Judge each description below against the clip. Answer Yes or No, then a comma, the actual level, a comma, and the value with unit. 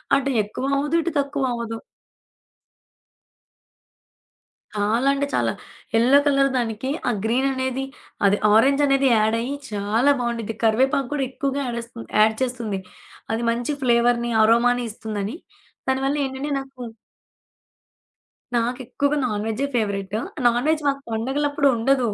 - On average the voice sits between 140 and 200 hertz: No, high, 245 Hz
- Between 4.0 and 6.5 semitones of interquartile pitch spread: No, average, 3.3 semitones